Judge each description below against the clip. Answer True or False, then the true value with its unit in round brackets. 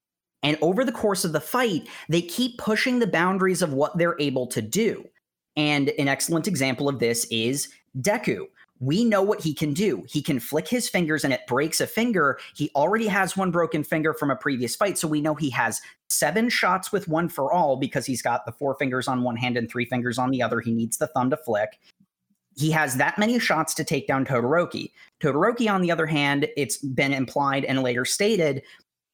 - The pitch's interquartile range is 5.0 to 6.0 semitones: True (5.4 semitones)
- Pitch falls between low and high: True (150 Hz)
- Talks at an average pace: False (215 wpm)